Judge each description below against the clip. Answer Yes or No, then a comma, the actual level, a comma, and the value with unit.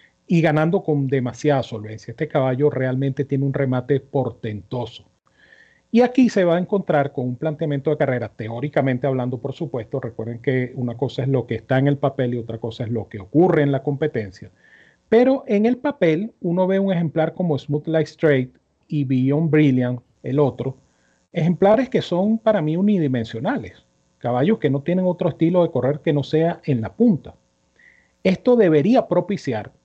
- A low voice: No, medium, 145 Hz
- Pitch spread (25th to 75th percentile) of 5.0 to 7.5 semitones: Yes, wide, 5.4 semitones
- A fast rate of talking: No, average, 175 wpm